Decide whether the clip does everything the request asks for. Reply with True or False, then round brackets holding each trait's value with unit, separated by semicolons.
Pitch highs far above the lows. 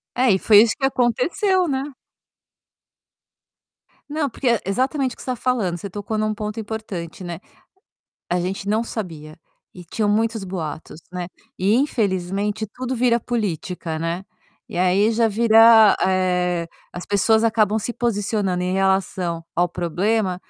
False (4.2 semitones)